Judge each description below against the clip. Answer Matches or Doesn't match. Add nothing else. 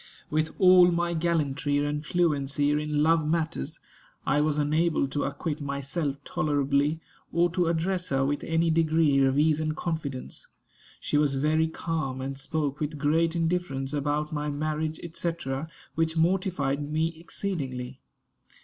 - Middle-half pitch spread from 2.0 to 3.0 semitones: Matches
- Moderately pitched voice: Matches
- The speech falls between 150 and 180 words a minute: Doesn't match